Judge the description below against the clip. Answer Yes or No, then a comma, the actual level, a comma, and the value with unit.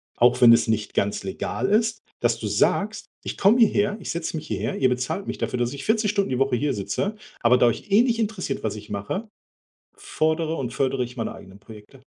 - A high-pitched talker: No, low, 135 Hz